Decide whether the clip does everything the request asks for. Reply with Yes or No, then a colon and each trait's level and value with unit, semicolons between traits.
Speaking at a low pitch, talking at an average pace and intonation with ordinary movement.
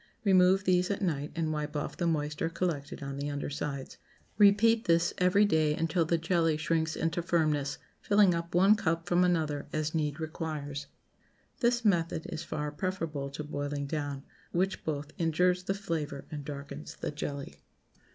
No: medium, 160 Hz; average, 165 wpm; average, 3.4 semitones